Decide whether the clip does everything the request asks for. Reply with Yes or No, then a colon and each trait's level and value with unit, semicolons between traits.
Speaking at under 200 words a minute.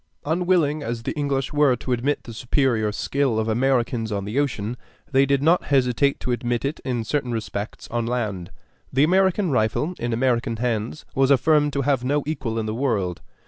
Yes: average, 185 wpm